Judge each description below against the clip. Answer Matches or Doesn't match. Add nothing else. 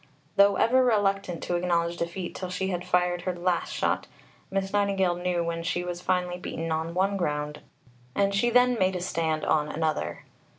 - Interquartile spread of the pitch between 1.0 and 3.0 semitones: Matches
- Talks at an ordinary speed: Matches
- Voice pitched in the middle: Matches